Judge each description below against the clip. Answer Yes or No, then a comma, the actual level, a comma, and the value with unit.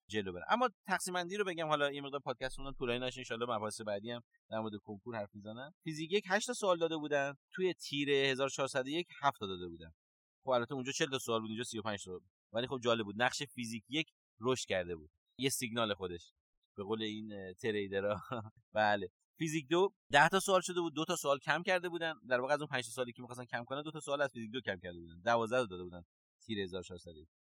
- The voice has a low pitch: Yes, low, 125 Hz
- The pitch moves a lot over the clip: Yes, wide, 6.1 semitones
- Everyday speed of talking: No, fast, 230 wpm